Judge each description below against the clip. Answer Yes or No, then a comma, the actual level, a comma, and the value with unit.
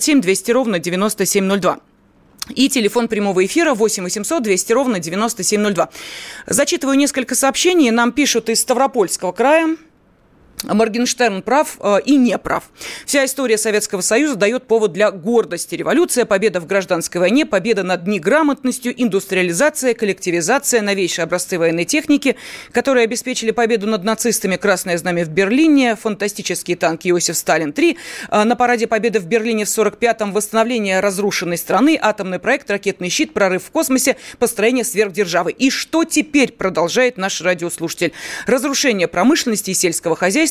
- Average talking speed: Yes, average, 135 wpm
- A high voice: Yes, high, 220 Hz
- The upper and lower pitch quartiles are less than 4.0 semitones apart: No, average, 5.0 semitones